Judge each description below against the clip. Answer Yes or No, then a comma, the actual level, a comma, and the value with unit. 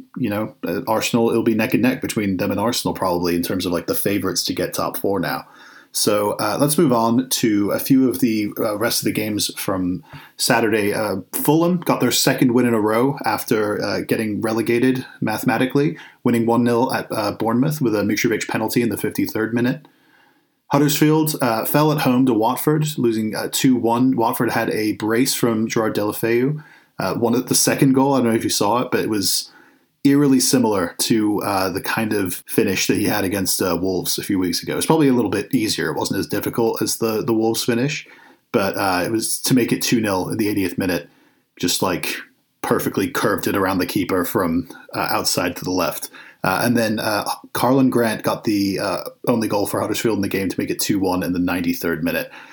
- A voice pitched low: Yes, low, 115 Hz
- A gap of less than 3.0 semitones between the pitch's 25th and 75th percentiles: No, average, 3.3 semitones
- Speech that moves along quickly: Yes, fast, 215 wpm